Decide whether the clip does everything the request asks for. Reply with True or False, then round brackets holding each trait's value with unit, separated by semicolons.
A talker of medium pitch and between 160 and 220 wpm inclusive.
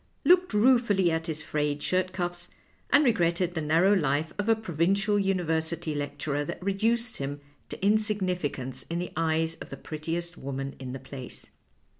True (170 Hz; 170 wpm)